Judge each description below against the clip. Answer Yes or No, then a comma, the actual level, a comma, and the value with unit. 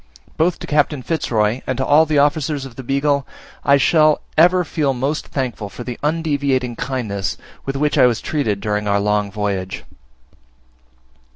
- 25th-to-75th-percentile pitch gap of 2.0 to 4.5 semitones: No, average, 5.0 semitones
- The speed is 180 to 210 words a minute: No, average, 170 wpm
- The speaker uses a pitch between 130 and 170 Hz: Yes, low, 135 Hz